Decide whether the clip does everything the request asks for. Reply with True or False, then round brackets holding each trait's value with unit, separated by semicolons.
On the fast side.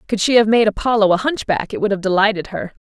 True (255 wpm)